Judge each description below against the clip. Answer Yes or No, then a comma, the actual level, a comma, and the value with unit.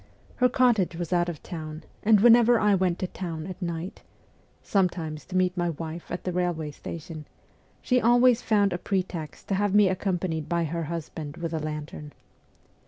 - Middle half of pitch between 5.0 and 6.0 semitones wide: No, average, 3.4 semitones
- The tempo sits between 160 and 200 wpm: Yes, average, 175 wpm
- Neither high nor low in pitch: Yes, medium, 175 Hz